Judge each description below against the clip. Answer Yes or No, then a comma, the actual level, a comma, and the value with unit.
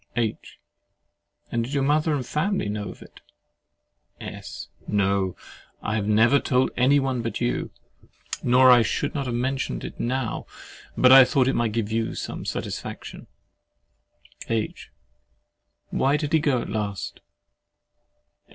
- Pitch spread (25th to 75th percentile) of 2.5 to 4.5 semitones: Yes, average, 3.5 semitones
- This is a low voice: Yes, low, 125 Hz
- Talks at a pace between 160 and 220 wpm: No, average, 140 wpm